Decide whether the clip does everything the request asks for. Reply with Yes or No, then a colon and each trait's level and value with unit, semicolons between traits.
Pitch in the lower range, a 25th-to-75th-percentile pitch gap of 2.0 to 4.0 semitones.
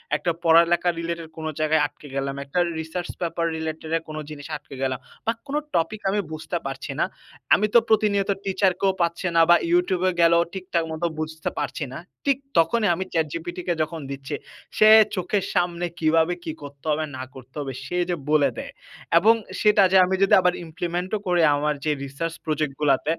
No: medium, 165 Hz; average, 2.9 semitones